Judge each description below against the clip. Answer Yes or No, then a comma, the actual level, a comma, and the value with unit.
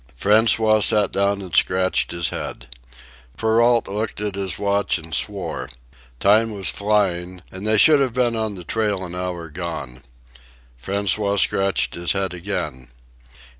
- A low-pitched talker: Yes, low, 100 Hz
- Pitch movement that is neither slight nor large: Yes, average, 3.1 semitones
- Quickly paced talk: No, average, 145 wpm